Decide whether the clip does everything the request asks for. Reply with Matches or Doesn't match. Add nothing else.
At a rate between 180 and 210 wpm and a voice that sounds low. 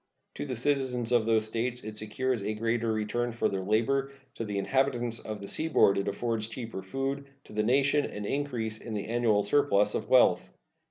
Matches